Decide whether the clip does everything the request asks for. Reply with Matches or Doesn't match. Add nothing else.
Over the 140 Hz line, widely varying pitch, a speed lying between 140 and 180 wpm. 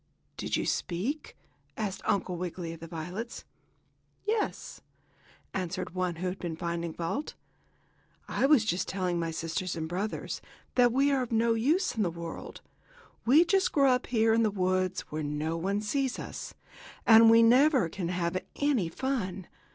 Matches